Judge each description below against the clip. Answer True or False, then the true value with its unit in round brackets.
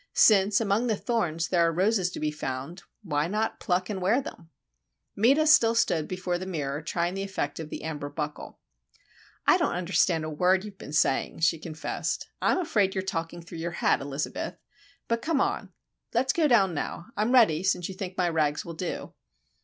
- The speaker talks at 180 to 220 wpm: True (190 wpm)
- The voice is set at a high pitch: False (180 Hz)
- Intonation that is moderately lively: True (4.4 semitones)